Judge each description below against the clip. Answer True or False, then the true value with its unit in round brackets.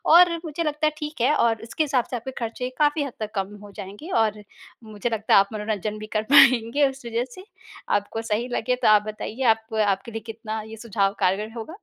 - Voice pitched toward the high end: True (225 Hz)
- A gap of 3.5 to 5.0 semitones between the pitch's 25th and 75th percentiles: True (3.9 semitones)